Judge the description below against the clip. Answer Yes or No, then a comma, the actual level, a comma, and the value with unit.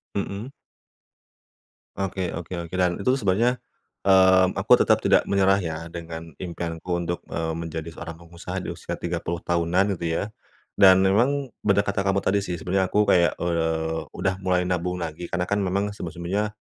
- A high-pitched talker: No, very low, 90 Hz